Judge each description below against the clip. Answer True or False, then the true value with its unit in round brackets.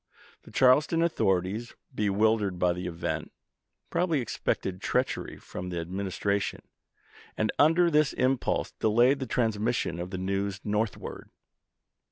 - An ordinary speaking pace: False (130 wpm)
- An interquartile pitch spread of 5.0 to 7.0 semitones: True (5.4 semitones)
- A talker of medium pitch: False (105 Hz)